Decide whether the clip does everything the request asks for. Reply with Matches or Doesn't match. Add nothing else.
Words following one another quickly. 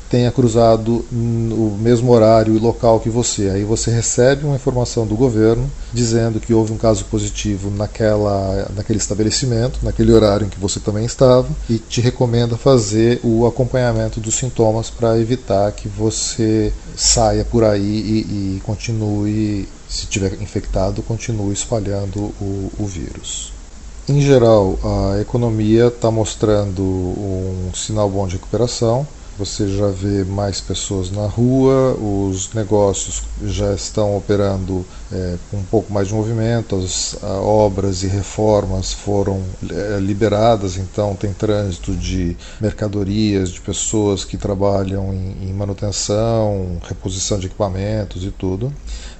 Doesn't match